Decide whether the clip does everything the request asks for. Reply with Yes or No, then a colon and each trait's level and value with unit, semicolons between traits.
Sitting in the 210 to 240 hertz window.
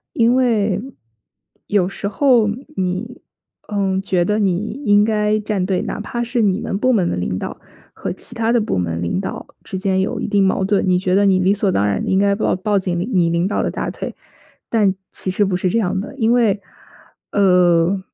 No: high, 200 Hz